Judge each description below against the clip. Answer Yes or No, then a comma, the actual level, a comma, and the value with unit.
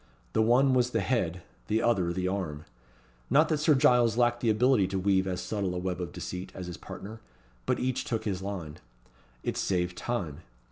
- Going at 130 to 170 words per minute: No, average, 195 wpm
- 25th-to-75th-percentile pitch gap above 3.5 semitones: Yes, average, 4.9 semitones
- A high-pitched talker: No, low, 100 Hz